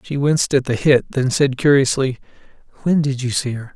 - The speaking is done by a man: Yes, male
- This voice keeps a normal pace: No, fast, 210 wpm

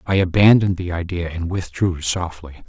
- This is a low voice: Yes, very low, 90 Hz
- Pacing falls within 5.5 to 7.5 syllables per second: No, 5.3 syllables/s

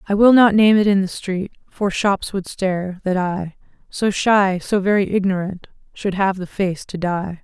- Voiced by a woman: Yes, female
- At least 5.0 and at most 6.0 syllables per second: No, 4.5 syllables/s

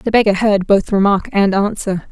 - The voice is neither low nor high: No, high, 200 Hz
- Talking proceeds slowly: No, average, 200 wpm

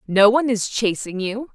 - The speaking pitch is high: Yes, high, 220 Hz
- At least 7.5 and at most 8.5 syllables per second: No, 5.0 syllables/s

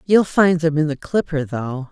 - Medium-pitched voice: Yes, medium, 155 Hz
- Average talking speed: No, fast, 220 wpm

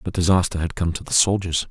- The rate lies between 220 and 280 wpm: Yes, fast, 245 wpm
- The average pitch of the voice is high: No, very low, 90 Hz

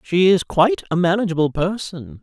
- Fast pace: No, average, 160 wpm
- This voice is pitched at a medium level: Yes, medium, 170 Hz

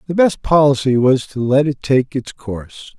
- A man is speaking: Yes, male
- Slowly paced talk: No, average, 200 wpm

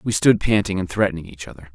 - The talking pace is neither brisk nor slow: No, fast, 240 wpm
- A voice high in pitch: No, very low, 90 Hz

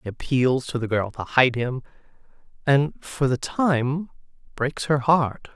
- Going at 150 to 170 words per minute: Yes, average, 160 wpm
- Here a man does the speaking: Yes, male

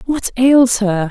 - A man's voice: No, female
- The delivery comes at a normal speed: Yes, average, 160 wpm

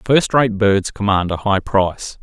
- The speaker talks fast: No, average, 190 wpm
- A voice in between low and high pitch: No, low, 105 Hz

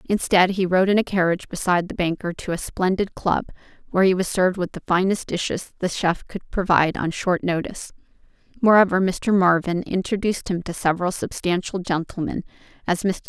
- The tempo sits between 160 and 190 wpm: Yes, average, 175 wpm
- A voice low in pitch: No, medium, 185 Hz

